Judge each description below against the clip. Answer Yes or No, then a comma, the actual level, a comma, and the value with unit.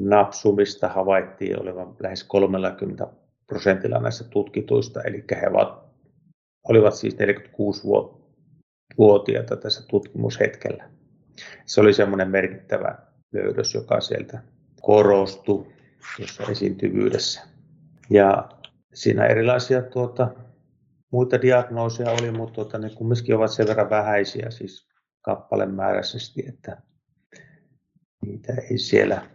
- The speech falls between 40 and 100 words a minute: Yes, slow, 95 wpm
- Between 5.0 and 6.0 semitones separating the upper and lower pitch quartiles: No, average, 4.1 semitones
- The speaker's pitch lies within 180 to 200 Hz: No, low, 115 Hz